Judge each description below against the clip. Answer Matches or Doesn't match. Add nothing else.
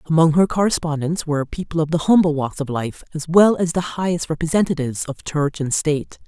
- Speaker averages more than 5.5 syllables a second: Matches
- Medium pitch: Matches